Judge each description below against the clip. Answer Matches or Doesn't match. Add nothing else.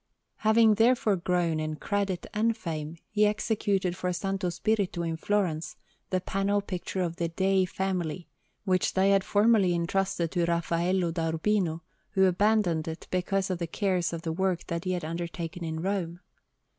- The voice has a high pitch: Doesn't match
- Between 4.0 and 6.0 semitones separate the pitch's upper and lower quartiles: Doesn't match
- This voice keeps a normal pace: Matches